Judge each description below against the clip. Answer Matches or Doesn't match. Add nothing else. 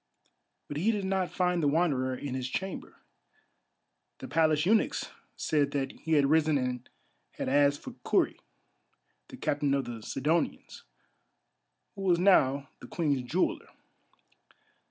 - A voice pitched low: Doesn't match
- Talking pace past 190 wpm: Doesn't match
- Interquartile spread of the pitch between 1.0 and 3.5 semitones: Doesn't match